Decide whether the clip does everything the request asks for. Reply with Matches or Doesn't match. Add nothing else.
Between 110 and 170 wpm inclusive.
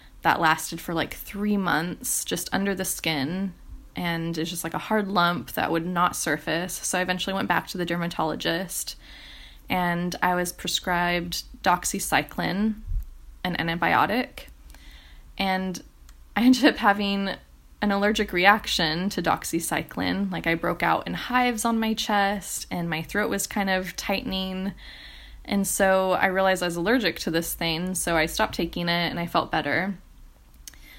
Matches